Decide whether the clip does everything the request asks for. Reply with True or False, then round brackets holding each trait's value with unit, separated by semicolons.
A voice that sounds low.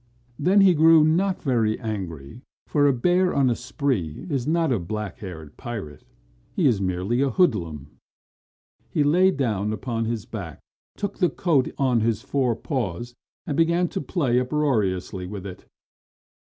True (120 Hz)